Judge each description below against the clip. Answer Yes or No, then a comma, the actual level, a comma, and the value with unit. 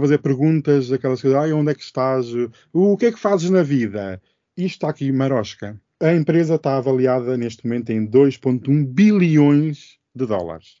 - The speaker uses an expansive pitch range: No, average, 3.6 semitones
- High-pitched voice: No, low, 135 Hz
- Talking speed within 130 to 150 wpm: No, average, 170 wpm